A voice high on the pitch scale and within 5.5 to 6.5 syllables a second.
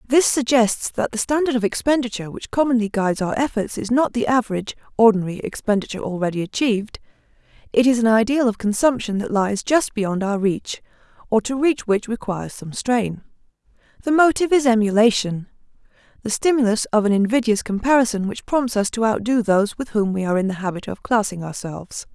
Yes: high, 225 Hz; 6.0 syllables/s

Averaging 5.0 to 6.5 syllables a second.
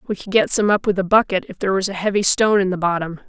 No: 7.0 syllables/s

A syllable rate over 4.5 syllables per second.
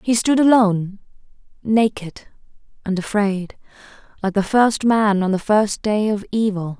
No: 4.4 syllables/s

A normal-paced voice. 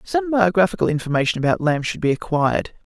Yes: average, 165 wpm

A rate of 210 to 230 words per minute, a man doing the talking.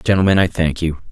Yes: fast, 215 wpm; male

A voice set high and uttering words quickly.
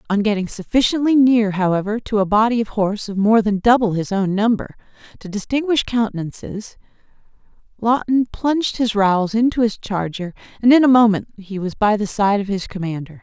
No: high, 215 Hz; average, 175 wpm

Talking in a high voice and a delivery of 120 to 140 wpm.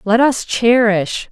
Yes: high, 220 Hz; slow, 135 wpm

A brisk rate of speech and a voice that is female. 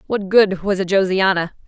No: average, 180 wpm; female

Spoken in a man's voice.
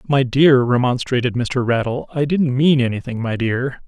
Yes: male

